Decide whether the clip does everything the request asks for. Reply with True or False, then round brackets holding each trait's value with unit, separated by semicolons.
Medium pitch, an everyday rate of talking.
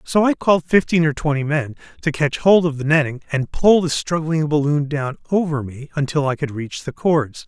False (150 Hz; 215 wpm)